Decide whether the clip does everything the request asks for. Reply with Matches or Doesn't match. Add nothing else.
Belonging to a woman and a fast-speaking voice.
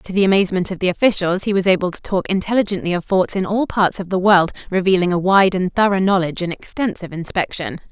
Matches